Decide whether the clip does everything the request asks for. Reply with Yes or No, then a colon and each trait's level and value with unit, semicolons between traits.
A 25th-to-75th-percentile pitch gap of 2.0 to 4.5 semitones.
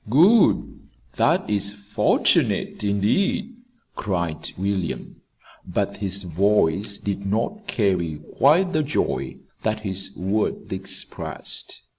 Yes: average, 3.2 semitones